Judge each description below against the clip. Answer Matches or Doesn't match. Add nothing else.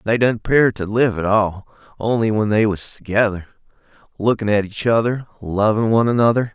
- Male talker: Matches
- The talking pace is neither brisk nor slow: Matches